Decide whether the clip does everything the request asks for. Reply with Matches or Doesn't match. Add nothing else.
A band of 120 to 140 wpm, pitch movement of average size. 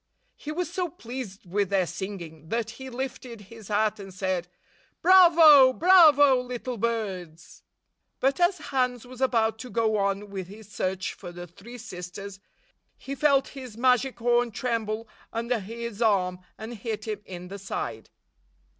Doesn't match